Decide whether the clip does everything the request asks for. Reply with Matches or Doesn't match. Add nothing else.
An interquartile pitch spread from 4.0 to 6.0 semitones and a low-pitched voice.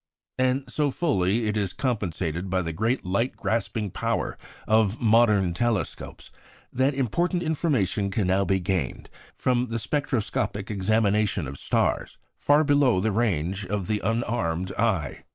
Matches